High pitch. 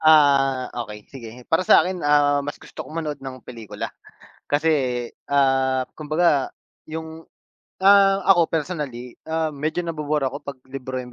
No: medium, 145 Hz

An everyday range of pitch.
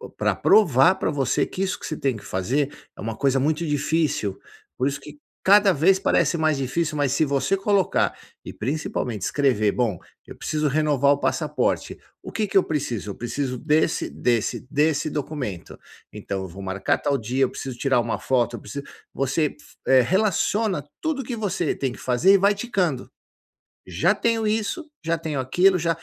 No: wide, 5.8 semitones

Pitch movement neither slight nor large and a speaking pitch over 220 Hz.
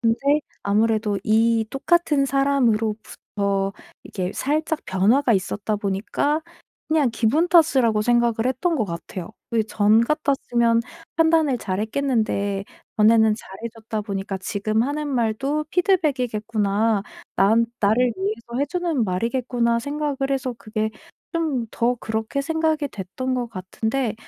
Yes: average, 4.5 semitones; high, 230 Hz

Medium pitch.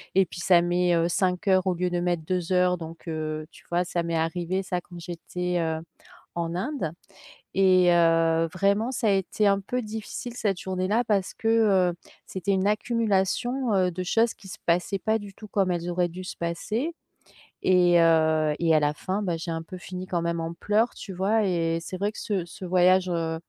Yes: medium, 180 Hz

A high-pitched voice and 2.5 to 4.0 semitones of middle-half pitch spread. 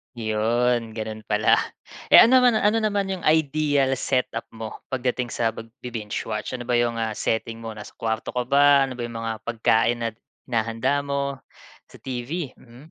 No: low, 120 Hz; average, 3.7 semitones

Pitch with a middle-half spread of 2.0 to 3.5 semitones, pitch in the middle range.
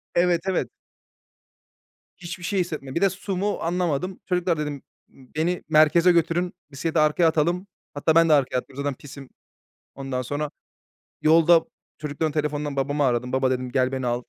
No: average, 3.9 semitones; medium, 155 Hz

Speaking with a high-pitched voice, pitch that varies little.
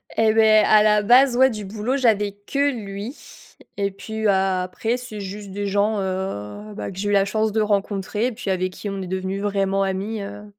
Yes: high, 205 Hz; narrow, 1.9 semitones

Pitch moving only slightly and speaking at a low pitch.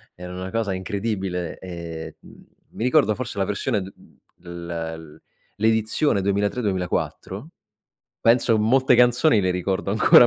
No: average, 4.0 semitones; low, 100 Hz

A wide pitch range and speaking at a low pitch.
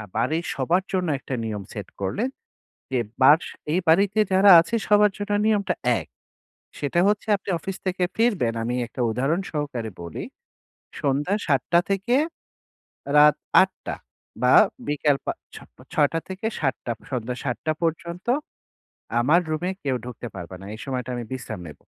No: wide, 6.9 semitones; medium, 150 Hz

